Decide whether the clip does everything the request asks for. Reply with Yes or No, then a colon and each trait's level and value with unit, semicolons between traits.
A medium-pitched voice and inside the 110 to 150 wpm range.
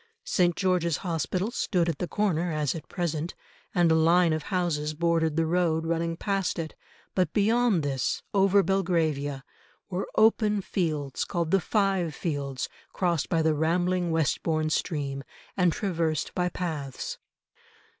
Yes: medium, 170 Hz; average, 145 wpm